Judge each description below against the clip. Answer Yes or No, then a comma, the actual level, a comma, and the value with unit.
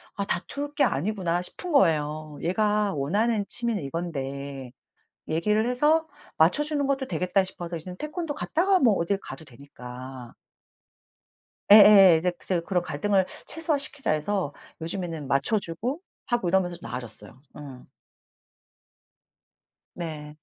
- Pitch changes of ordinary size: No, wide, 6.8 semitones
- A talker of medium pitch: Yes, medium, 180 Hz